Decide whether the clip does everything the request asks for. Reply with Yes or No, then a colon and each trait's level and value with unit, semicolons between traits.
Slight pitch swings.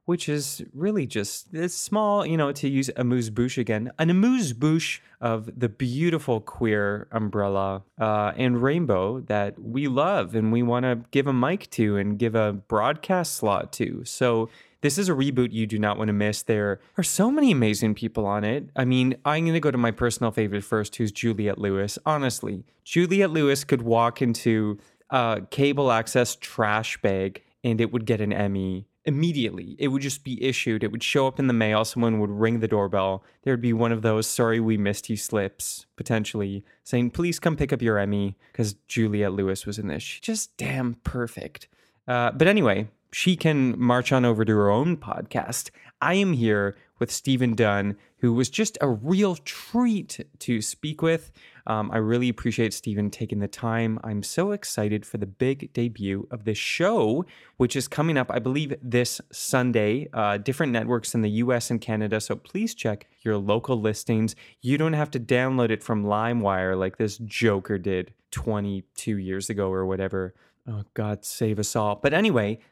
No: average, 4.2 semitones